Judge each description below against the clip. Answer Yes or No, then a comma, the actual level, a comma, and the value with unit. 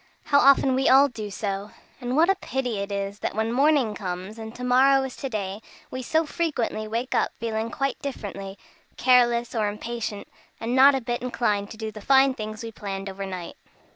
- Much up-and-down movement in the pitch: No, average, 4.2 semitones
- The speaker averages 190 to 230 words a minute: Yes, average, 200 wpm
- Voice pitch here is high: Yes, high, 230 Hz